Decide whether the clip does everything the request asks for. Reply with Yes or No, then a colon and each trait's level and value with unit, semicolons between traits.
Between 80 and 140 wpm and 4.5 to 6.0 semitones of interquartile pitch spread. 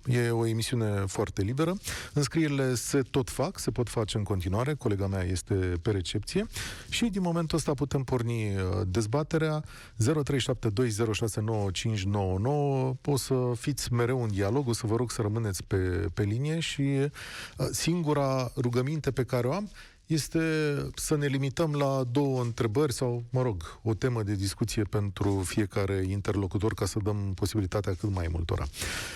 No: average, 150 wpm; average, 5.1 semitones